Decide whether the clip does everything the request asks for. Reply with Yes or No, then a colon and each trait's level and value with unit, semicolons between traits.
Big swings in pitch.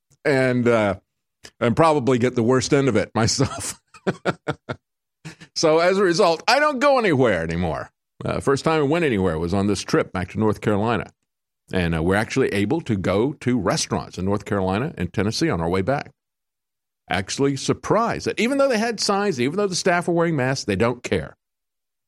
Yes: wide, 8.2 semitones